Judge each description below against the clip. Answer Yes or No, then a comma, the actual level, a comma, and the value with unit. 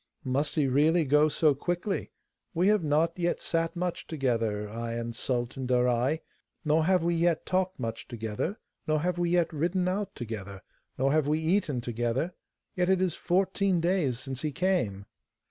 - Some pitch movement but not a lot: No, wide, 6.0 semitones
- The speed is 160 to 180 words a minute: Yes, average, 170 wpm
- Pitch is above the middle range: No, medium, 155 Hz